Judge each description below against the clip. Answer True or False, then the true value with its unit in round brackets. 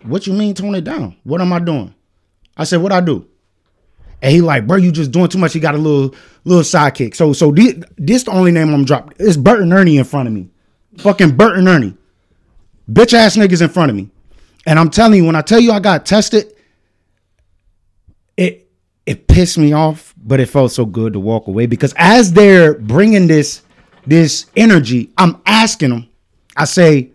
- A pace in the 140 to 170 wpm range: False (205 wpm)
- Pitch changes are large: True (8.7 semitones)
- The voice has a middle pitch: True (155 Hz)